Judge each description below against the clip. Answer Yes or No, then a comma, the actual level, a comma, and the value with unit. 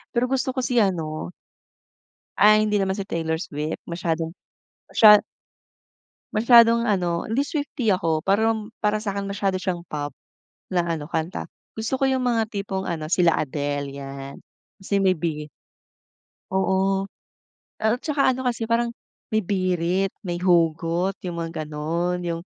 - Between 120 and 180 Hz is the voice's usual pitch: No, high, 190 Hz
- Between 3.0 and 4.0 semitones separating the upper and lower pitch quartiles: No, average, 4.8 semitones